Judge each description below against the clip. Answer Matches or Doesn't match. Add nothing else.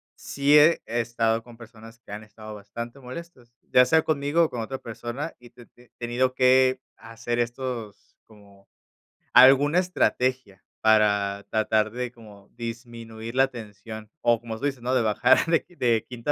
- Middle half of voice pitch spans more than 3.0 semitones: Doesn't match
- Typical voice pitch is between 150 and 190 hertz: Doesn't match